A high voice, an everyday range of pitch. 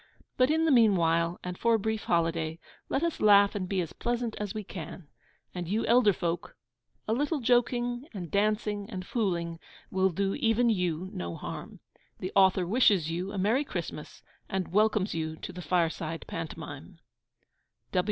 Yes: high, 195 Hz; average, 4.8 semitones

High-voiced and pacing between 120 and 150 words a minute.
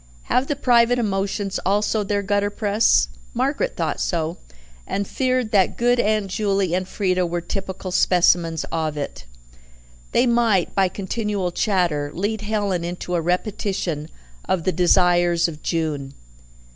Yes: high, 195 Hz; average, 140 wpm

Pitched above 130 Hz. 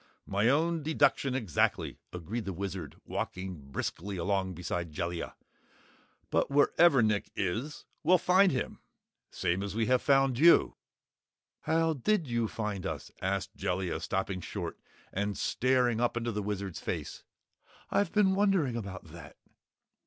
No: low, 110 Hz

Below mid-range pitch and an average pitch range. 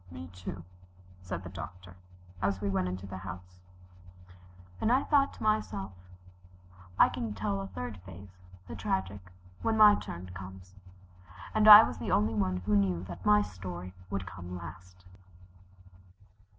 No: very low, 95 Hz; narrow, 2.0 semitones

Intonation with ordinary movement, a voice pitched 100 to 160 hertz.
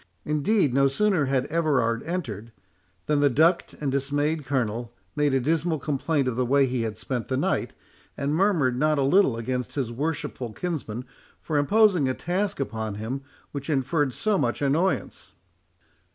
Yes: average, 4.0 semitones; medium, 140 Hz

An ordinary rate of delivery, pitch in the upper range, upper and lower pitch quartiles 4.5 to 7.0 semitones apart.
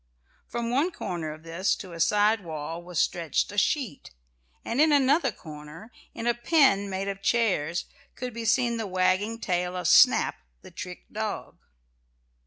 Yes: average, 165 wpm; high, 200 Hz; wide, 5.4 semitones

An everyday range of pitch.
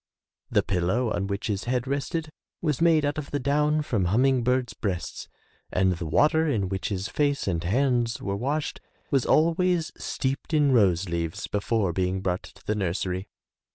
No: wide, 7.1 semitones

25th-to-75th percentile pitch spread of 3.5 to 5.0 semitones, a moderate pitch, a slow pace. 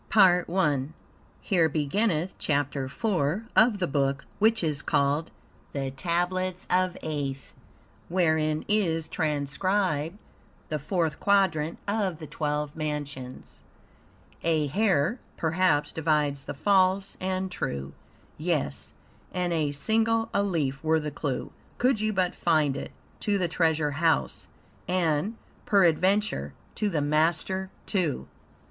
Yes: average, 4.2 semitones; medium, 165 Hz; slow, 120 wpm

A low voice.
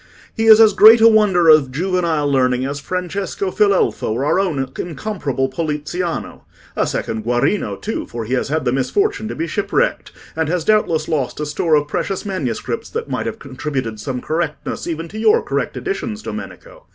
No: medium, 165 Hz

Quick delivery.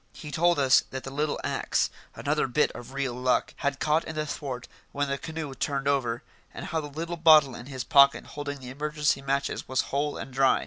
Yes: fast, 215 wpm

